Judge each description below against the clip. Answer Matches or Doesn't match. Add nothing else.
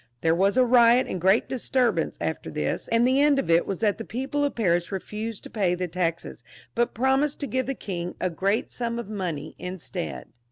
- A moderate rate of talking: Doesn't match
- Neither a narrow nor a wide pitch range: Doesn't match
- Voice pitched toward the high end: Matches